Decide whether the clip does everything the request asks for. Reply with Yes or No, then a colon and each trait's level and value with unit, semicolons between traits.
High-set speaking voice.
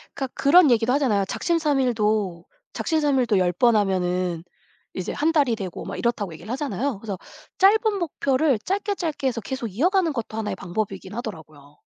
Yes: high, 235 Hz